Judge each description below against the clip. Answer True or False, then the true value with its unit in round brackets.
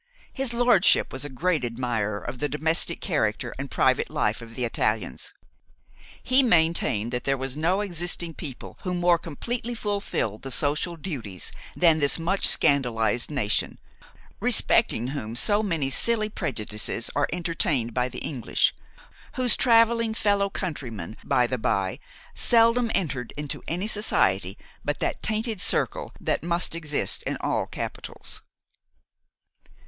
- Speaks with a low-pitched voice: False (155 Hz)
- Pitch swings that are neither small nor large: False (8.3 semitones)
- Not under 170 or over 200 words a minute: False (140 wpm)